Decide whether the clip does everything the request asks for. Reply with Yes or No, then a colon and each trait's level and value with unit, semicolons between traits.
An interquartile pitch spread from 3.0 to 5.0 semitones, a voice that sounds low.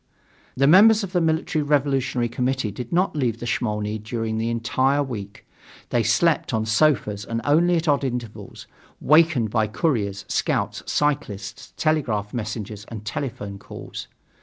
No: wide, 5.4 semitones; low, 120 Hz